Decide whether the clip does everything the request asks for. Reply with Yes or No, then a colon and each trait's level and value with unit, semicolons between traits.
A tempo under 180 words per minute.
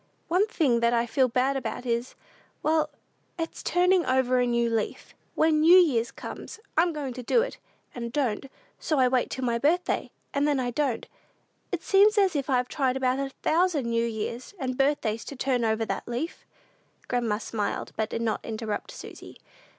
No: average, 185 wpm